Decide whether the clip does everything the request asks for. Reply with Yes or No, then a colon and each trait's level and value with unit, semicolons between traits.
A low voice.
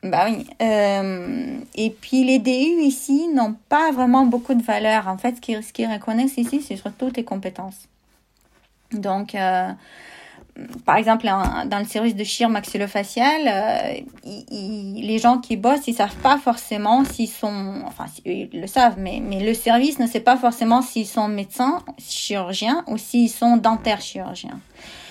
No: high, 230 Hz